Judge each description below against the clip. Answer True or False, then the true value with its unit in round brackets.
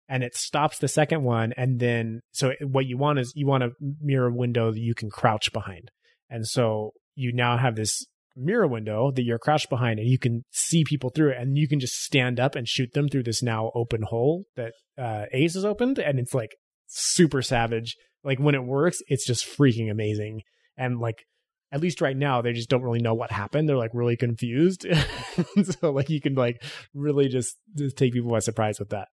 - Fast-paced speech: True (215 wpm)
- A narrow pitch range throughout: False (3.8 semitones)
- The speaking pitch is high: False (125 Hz)